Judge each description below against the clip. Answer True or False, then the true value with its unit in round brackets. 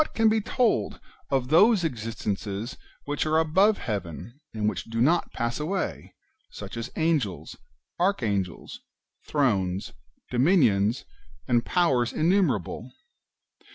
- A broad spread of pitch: True (7.7 semitones)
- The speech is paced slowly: True (115 wpm)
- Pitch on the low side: True (130 Hz)